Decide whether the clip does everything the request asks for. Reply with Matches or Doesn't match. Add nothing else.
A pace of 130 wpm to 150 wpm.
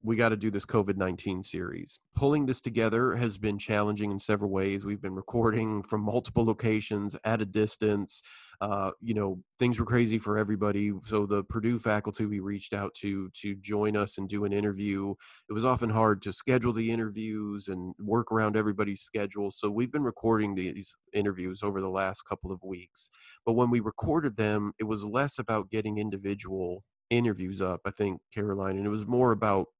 Doesn't match